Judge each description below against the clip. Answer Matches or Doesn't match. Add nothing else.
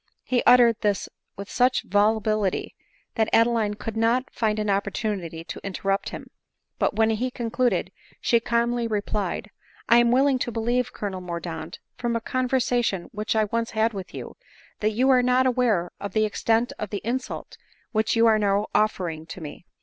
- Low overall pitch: Doesn't match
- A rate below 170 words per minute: Doesn't match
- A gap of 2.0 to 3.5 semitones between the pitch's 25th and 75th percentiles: Matches